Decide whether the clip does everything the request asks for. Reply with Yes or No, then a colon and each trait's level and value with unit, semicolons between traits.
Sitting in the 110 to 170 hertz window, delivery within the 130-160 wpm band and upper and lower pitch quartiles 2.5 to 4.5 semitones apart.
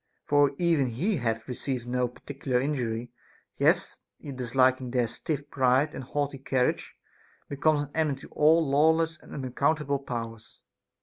Yes: low, 135 Hz; average, 145 wpm; average, 3.0 semitones